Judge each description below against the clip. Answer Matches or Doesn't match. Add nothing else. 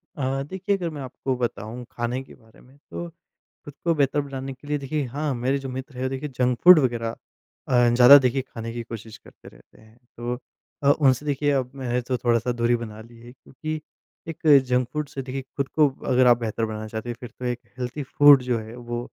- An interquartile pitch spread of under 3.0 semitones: Matches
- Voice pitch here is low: Matches